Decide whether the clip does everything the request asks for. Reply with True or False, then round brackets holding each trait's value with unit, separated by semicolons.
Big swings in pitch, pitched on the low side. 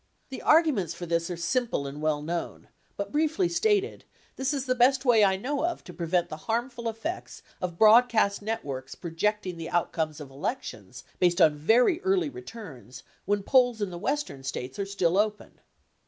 False (7.3 semitones; 205 Hz)